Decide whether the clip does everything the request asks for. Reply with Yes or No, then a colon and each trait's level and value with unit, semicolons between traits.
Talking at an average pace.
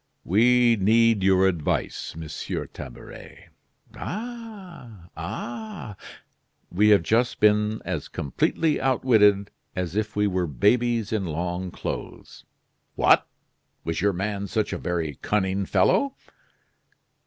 No: slow, 110 wpm